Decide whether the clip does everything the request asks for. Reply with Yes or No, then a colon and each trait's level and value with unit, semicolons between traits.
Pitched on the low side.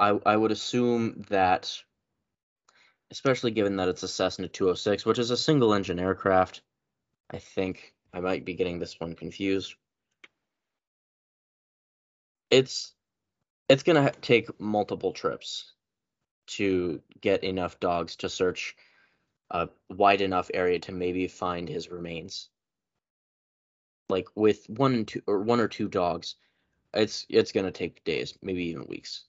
Yes: very low, 95 Hz